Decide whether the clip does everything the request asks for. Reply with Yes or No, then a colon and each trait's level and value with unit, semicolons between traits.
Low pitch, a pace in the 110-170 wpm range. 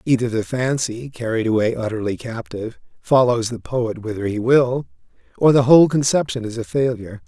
Yes: low, 120 Hz; average, 165 wpm